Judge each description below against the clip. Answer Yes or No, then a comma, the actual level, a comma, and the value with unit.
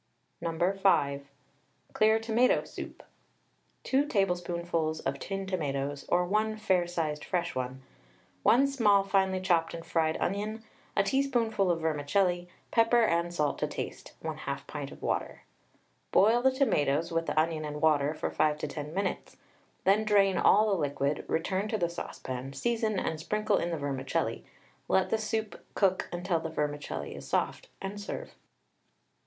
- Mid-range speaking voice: Yes, medium, 175 Hz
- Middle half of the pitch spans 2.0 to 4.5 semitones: No, wide, 5.4 semitones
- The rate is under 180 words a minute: Yes, average, 155 wpm